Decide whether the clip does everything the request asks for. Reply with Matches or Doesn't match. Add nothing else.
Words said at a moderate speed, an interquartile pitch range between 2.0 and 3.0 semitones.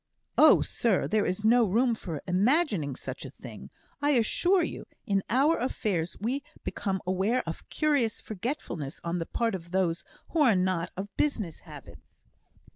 Doesn't match